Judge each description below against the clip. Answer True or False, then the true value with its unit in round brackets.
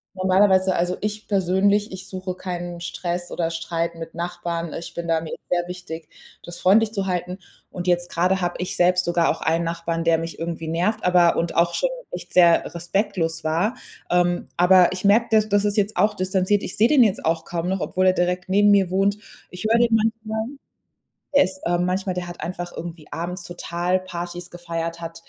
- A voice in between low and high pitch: True (180 Hz)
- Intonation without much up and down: True (2.0 semitones)